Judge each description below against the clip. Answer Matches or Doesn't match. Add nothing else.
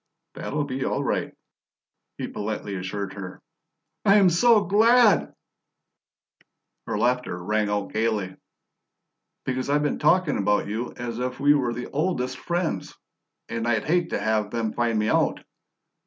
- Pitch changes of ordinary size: Doesn't match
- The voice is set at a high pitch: Doesn't match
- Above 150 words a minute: Doesn't match